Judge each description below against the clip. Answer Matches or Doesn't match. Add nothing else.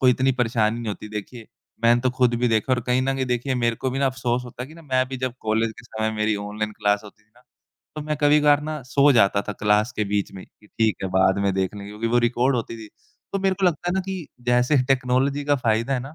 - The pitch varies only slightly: Doesn't match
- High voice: Doesn't match